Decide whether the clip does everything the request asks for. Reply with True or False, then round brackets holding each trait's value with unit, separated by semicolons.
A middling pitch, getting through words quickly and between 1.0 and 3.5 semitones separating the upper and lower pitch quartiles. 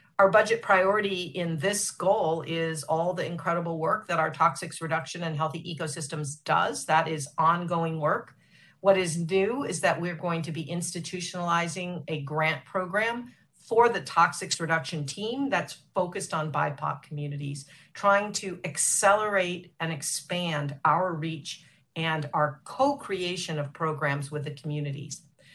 False (165 Hz; 145 wpm; 2.7 semitones)